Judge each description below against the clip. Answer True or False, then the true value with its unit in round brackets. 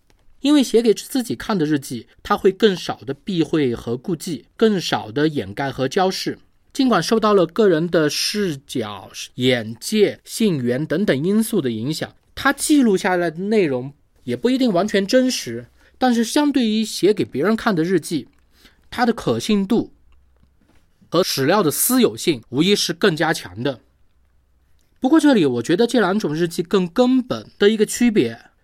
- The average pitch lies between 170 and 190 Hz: True (185 Hz)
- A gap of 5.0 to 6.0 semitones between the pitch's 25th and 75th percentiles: False (8.7 semitones)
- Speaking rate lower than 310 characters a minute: True (245 characters per minute)